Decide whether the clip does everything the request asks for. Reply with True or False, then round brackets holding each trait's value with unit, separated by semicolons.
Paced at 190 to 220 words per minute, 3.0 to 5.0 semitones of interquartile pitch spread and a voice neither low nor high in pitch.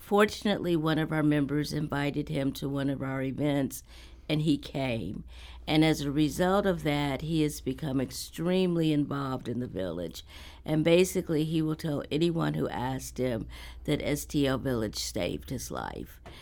False (160 wpm; 3.7 semitones; 145 Hz)